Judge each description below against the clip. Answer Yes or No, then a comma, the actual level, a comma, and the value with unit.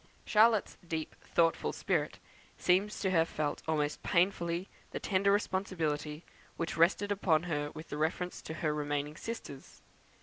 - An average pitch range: Yes, average, 3.8 semitones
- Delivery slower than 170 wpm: Yes, slow, 135 wpm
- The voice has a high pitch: No, medium, 165 Hz